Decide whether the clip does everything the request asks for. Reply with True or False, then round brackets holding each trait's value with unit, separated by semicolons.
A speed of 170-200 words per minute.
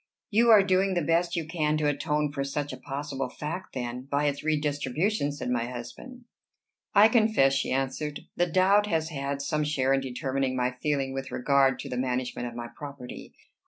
True (190 wpm)